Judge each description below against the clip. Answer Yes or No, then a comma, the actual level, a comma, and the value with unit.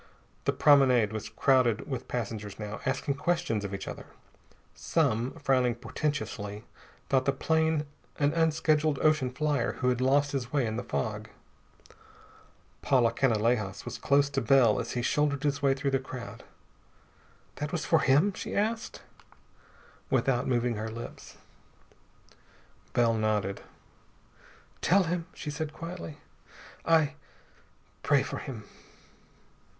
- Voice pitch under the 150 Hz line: Yes, low, 135 Hz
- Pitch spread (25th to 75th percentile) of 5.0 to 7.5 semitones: No, average, 4.4 semitones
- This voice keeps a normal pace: No, slow, 130 wpm